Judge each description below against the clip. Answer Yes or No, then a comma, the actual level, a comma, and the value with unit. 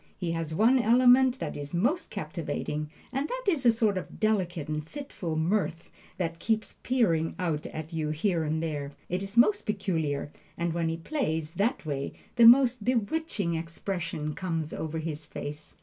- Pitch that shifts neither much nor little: No, wide, 6.5 semitones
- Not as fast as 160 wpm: No, average, 170 wpm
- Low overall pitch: No, medium, 170 Hz